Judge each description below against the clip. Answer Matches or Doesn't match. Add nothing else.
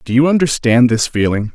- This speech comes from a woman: Doesn't match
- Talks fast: Doesn't match